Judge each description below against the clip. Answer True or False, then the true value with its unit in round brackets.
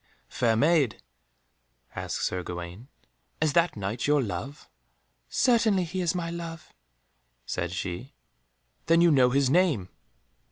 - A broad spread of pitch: True (7.9 semitones)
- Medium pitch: True (145 Hz)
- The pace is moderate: False (125 wpm)